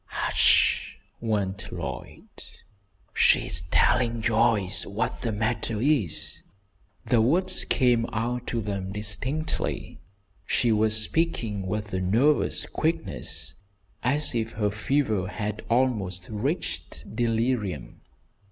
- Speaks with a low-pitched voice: Yes, low, 115 Hz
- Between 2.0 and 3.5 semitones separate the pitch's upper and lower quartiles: Yes, average, 3.2 semitones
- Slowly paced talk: Yes, slow, 105 wpm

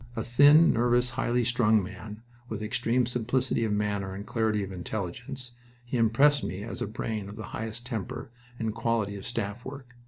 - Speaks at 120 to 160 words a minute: No, average, 180 wpm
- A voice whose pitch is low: Yes, low, 115 Hz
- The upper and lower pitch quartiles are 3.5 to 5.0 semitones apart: No, average, 2.7 semitones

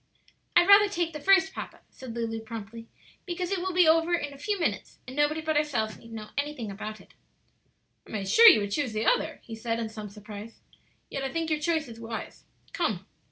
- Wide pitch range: Yes, wide, 7.0 semitones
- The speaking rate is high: Yes, fast, 215 wpm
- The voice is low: No, very high, 265 Hz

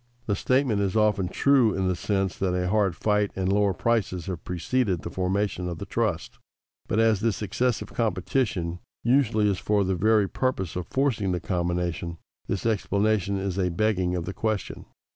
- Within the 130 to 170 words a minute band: No, average, 180 wpm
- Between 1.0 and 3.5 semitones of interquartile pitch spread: Yes, average, 3.1 semitones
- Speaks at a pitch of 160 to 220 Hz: No, low, 100 Hz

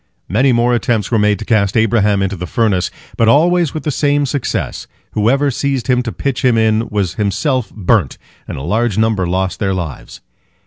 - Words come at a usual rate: Yes, average, 185 wpm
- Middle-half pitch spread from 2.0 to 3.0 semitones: No, average, 4.1 semitones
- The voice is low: Yes, low, 110 Hz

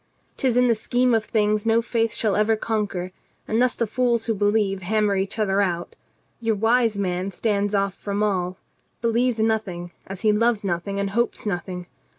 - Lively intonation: No, narrow, 2.6 semitones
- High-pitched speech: Yes, high, 210 Hz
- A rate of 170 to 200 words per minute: Yes, average, 180 wpm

